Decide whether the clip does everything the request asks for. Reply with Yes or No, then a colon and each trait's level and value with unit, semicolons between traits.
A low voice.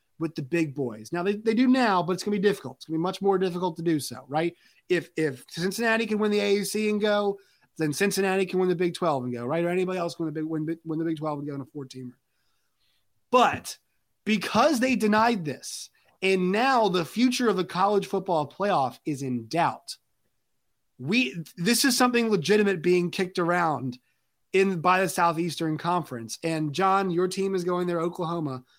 No: medium, 180 Hz